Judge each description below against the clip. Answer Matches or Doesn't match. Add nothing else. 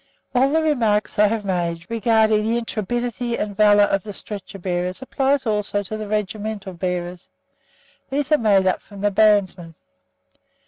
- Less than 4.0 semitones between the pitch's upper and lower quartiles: Matches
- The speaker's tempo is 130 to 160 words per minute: Matches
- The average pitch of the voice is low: Doesn't match